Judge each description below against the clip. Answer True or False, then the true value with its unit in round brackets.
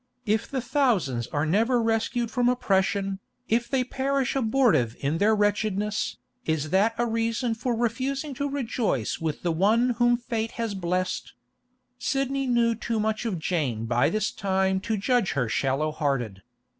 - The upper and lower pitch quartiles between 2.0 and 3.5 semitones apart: False (5.4 semitones)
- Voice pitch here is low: False (220 Hz)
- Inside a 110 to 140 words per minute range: False (155 wpm)